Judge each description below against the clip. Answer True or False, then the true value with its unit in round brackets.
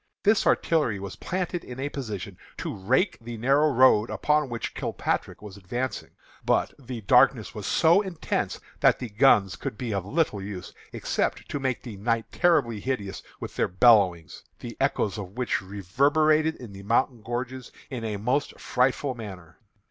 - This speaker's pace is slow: False (165 wpm)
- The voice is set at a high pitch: False (120 Hz)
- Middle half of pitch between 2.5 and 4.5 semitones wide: False (5.1 semitones)